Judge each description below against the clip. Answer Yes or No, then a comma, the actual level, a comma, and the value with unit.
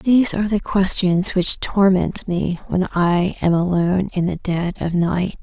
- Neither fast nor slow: Yes, average, 175 wpm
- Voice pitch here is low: No, medium, 185 Hz